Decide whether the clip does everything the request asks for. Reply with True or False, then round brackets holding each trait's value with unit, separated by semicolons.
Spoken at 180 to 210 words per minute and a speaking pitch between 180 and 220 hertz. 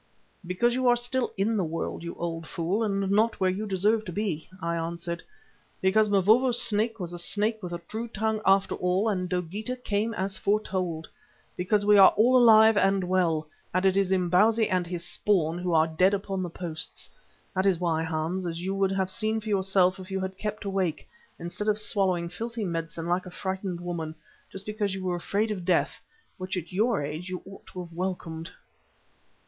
True (200 wpm; 190 Hz)